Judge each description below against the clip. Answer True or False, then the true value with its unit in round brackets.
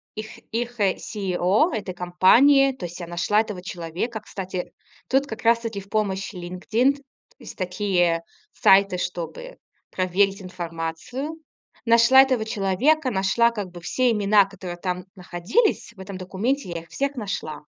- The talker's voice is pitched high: True (195 Hz)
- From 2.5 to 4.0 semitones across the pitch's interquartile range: False (4.5 semitones)